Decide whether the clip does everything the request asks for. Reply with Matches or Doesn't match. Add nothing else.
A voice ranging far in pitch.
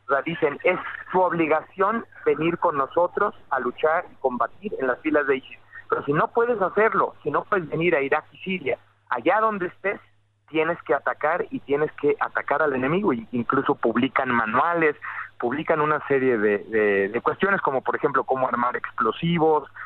Matches